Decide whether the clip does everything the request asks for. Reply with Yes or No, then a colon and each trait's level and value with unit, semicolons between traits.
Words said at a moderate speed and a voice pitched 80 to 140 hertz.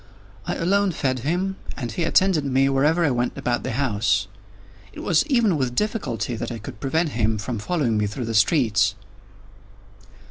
Yes: average, 175 wpm; low, 135 Hz